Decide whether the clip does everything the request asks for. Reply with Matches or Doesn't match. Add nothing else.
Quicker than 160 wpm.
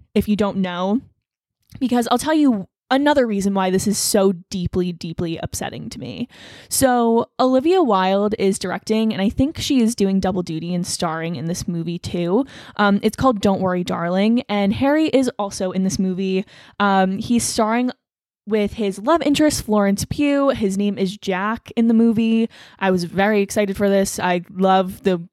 Matches